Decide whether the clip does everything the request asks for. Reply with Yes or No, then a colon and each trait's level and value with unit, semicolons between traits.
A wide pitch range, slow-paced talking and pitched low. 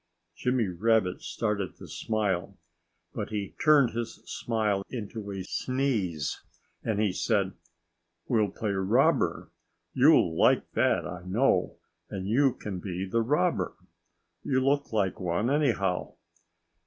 No: average, 3.9 semitones; slow, 125 wpm; low, 105 Hz